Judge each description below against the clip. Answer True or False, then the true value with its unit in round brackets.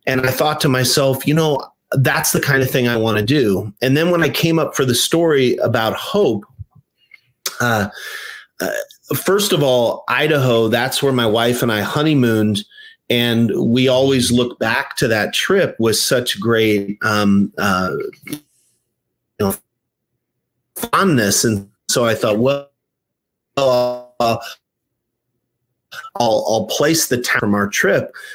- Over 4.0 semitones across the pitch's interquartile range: True (4.4 semitones)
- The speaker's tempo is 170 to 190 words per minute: False (150 wpm)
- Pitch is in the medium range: False (125 Hz)